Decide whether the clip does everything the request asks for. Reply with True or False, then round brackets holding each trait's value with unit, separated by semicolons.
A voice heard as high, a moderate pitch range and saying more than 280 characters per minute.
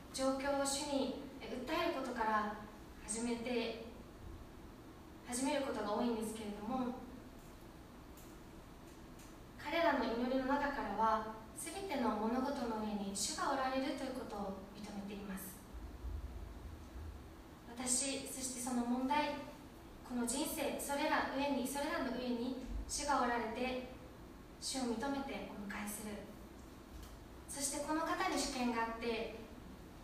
False (250 Hz; 4.5 semitones; 235 characters per minute)